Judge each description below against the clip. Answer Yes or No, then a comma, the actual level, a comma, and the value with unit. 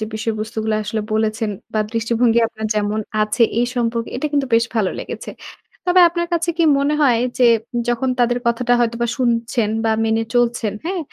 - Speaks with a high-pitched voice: Yes, high, 230 Hz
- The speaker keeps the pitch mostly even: Yes, narrow, 2.0 semitones